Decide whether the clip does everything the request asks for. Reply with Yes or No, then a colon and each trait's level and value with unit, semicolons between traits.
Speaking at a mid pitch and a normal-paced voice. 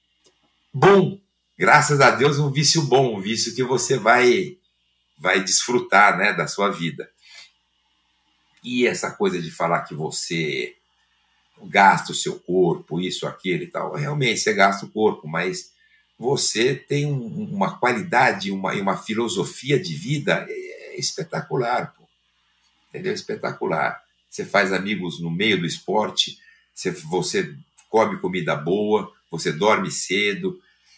Yes: medium, 160 Hz; average, 130 wpm